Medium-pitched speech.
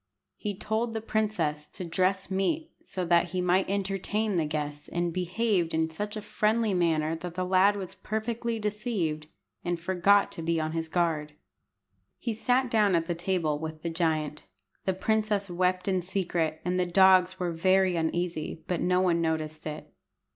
Yes: medium, 180 Hz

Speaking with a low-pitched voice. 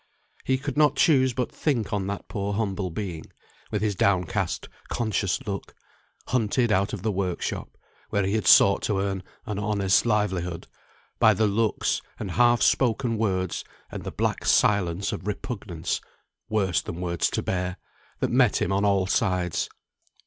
Yes: low, 100 Hz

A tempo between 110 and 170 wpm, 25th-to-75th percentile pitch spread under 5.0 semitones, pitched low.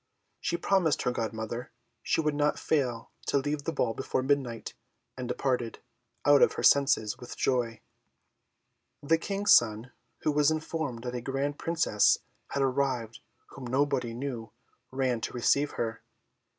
Yes: average, 150 wpm; average, 3.5 semitones; low, 130 Hz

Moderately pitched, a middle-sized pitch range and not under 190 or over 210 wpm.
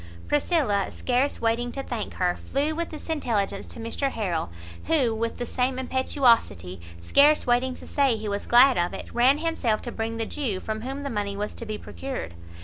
No: high, 240 Hz; average, 4.2 semitones; average, 195 wpm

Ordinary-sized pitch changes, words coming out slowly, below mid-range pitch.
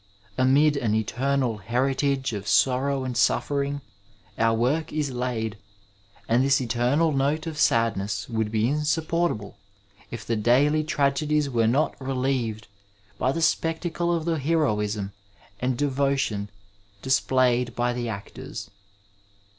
Yes: average, 4.1 semitones; slow, 125 wpm; low, 130 Hz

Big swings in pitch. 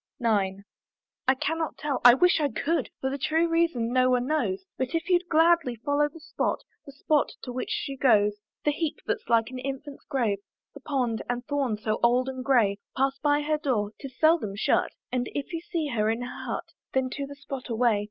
No: average, 3.7 semitones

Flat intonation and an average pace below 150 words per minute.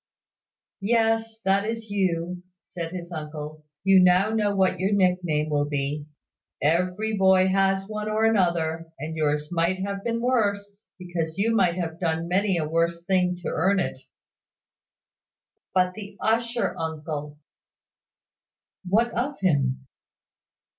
No: average, 3.9 semitones; slow, 135 wpm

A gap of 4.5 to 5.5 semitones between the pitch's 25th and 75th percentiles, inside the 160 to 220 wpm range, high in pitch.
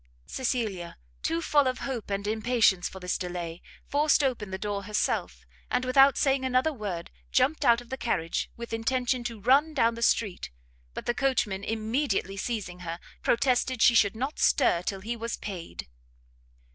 Yes: average, 4.9 semitones; average, 170 wpm; high, 230 Hz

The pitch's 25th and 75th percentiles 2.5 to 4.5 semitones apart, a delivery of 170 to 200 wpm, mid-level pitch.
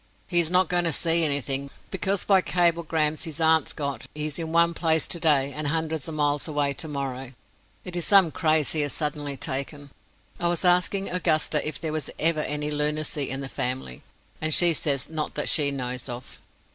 Yes: average, 2.9 semitones; average, 190 wpm; medium, 155 Hz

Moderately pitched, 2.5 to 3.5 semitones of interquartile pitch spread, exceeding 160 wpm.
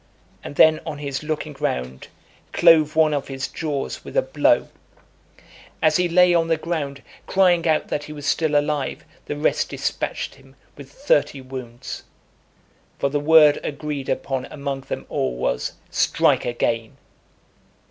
No: medium, 145 Hz; average, 2.8 semitones; average, 150 wpm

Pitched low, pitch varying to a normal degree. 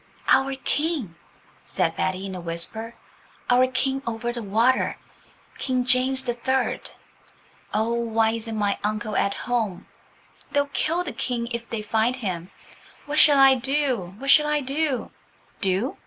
No: high, 240 Hz; average, 3.7 semitones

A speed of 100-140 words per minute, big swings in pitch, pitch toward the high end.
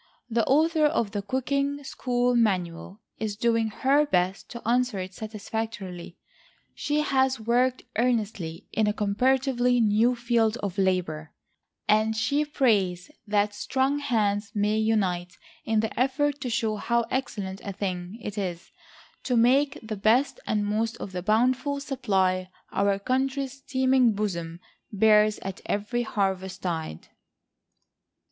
No: slow, 135 wpm; average, 4.4 semitones; high, 220 Hz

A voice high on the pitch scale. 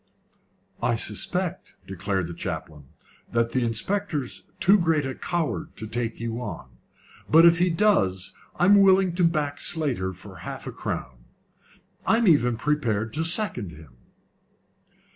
No: low, 130 Hz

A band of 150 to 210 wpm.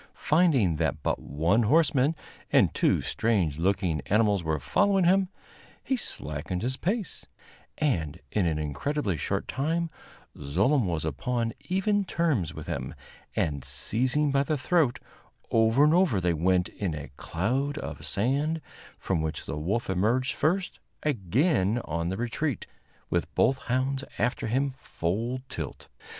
No: average, 140 wpm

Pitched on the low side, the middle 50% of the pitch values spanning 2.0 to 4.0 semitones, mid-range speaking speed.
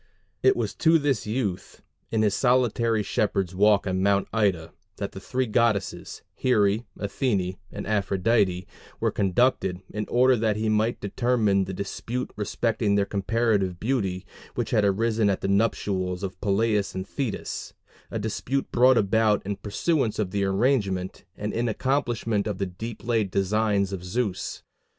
Yes: low, 105 Hz; average, 2.9 semitones; average, 155 wpm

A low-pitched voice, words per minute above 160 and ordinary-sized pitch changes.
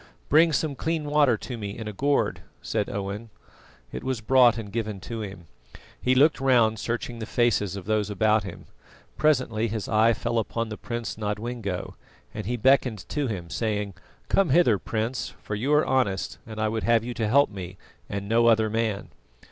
Yes: low, 115 Hz; average, 190 wpm; average, 3.1 semitones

